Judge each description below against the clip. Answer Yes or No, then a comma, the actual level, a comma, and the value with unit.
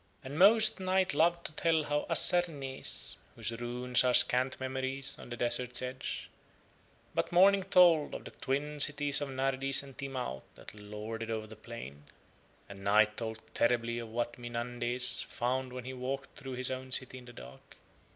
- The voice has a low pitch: Yes, low, 130 Hz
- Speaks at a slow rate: No, average, 170 wpm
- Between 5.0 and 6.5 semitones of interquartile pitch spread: No, average, 3.1 semitones